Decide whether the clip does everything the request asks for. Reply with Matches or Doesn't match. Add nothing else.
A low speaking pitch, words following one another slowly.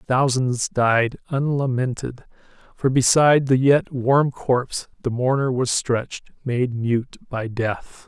Matches